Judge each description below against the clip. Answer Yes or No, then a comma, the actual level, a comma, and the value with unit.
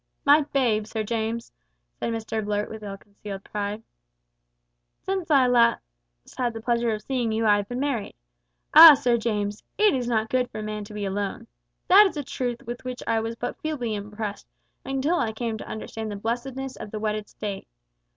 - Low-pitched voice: No, high, 225 Hz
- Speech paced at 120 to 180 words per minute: No, average, 190 wpm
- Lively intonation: No, average, 3.1 semitones